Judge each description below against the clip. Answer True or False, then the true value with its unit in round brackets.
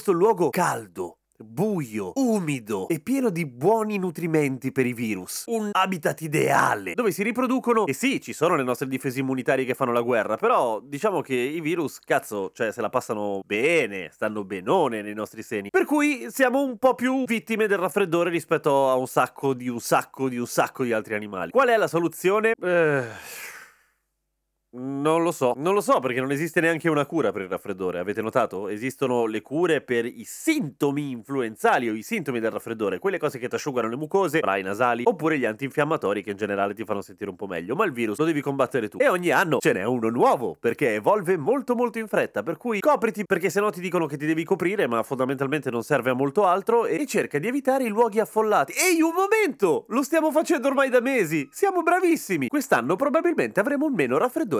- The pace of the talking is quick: True (205 wpm)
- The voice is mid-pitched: True (165 Hz)